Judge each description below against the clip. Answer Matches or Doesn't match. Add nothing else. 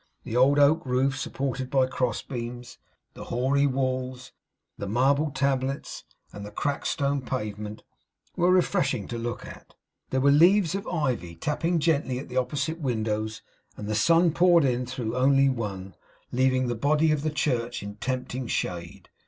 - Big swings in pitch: Doesn't match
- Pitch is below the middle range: Matches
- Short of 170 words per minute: Matches